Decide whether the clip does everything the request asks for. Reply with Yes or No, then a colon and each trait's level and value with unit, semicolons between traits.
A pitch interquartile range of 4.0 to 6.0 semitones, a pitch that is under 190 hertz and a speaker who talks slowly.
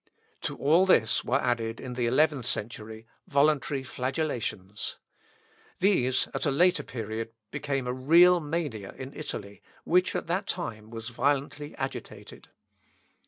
Yes: average, 5.0 semitones; low, 135 Hz; slow, 130 wpm